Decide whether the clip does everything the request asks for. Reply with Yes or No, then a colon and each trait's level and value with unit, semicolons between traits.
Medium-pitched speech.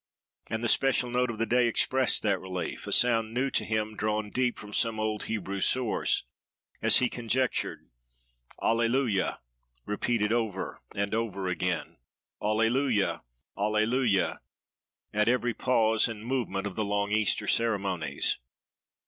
No: low, 110 Hz